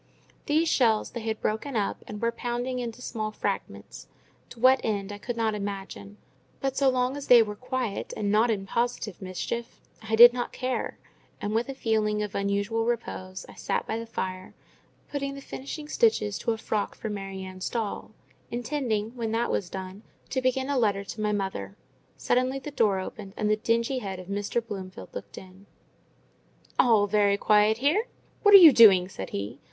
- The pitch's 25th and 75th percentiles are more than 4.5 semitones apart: No, average, 3.7 semitones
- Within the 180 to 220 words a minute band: Yes, average, 190 wpm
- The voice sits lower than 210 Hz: No, high, 220 Hz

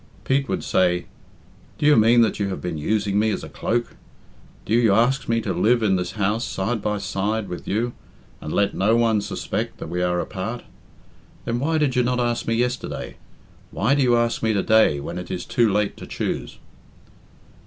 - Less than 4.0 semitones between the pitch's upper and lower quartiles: Yes, average, 3.6 semitones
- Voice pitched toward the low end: Yes, low, 110 Hz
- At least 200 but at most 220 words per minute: Yes, fast, 205 wpm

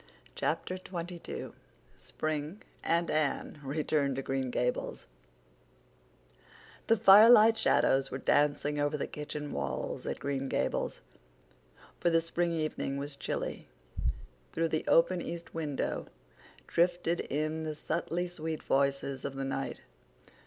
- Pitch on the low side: No, medium, 155 Hz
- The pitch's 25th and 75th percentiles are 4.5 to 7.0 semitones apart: No, average, 3.5 semitones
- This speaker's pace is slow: Yes, slow, 120 wpm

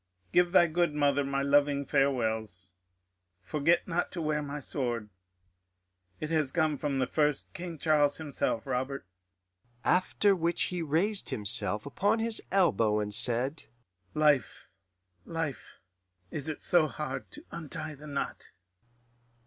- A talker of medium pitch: Yes, medium, 145 Hz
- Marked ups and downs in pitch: No, average, 3.9 semitones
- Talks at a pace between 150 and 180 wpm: No, slow, 135 wpm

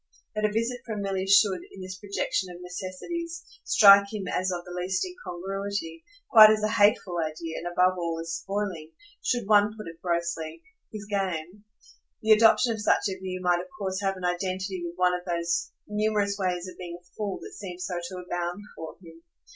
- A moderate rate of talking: Yes, average, 195 wpm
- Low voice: No, medium, 185 Hz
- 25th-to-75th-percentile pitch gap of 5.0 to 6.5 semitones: No, average, 2.8 semitones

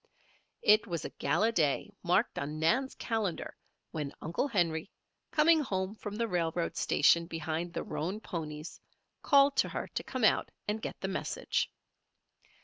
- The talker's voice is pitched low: No, medium, 185 Hz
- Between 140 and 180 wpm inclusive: Yes, average, 150 wpm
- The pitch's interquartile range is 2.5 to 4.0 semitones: No, wide, 5.4 semitones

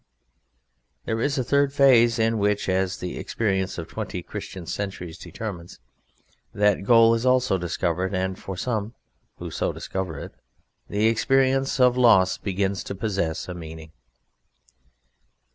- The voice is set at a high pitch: No, low, 100 Hz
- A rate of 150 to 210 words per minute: No, average, 140 wpm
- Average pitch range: Yes, average, 4.0 semitones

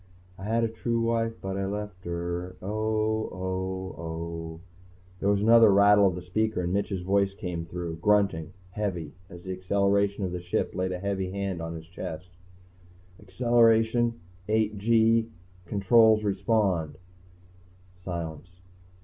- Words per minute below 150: Yes, average, 140 wpm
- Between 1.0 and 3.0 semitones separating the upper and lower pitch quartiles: No, average, 3.4 semitones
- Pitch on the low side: Yes, low, 100 Hz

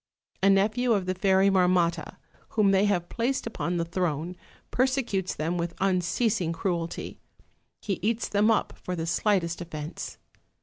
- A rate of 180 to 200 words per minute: No, average, 145 wpm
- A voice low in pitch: No, medium, 185 Hz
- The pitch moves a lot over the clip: No, average, 3.3 semitones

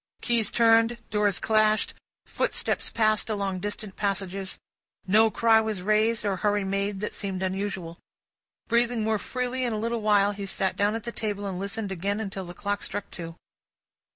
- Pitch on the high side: Yes, high, 205 Hz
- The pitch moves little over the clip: Yes, narrow, 2.2 semitones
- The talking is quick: No, average, 170 wpm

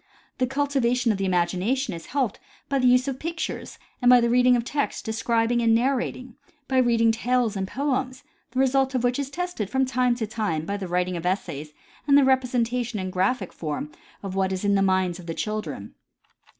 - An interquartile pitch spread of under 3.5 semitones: No, average, 5.1 semitones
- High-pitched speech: Yes, high, 235 Hz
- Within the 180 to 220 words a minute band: Yes, average, 200 wpm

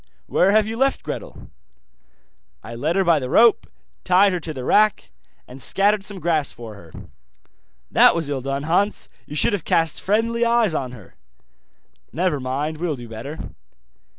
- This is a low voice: No, medium, 165 Hz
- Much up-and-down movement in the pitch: Yes, wide, 6.9 semitones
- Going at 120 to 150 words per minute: No, average, 170 wpm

